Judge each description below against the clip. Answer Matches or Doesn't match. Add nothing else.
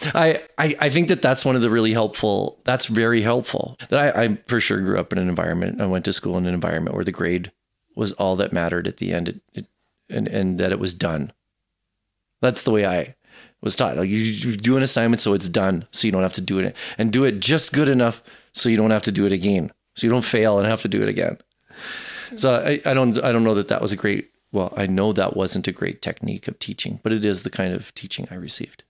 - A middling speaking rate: Doesn't match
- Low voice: Matches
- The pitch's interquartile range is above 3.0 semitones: Matches